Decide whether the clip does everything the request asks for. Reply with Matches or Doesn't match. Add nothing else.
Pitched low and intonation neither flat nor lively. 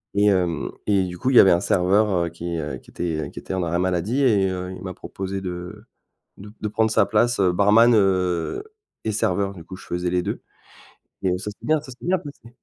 Matches